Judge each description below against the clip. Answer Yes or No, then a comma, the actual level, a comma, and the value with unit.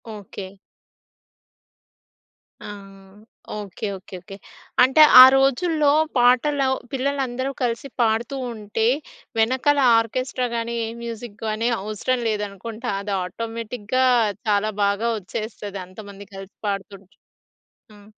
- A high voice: Yes, high, 225 Hz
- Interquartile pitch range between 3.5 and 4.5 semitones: Yes, average, 3.8 semitones